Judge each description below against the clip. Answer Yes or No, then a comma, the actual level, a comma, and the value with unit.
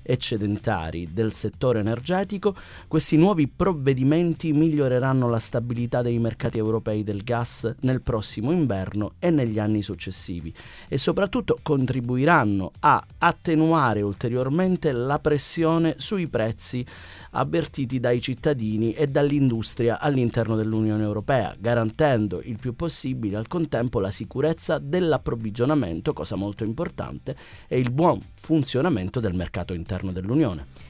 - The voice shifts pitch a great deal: Yes, wide, 6.1 semitones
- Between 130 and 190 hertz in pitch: No, low, 120 Hz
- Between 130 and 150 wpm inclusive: No, slow, 115 wpm